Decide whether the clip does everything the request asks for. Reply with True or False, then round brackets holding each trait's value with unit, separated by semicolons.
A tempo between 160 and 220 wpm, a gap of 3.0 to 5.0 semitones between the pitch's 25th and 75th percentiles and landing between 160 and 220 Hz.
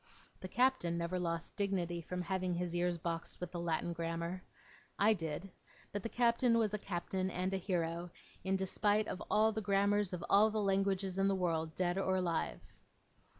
False (185 wpm; 2.6 semitones; 185 Hz)